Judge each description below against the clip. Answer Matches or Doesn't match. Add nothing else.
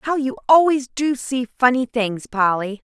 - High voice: Matches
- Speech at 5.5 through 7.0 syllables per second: Doesn't match